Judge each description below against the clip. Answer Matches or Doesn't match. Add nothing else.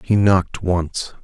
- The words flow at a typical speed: Matches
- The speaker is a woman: Doesn't match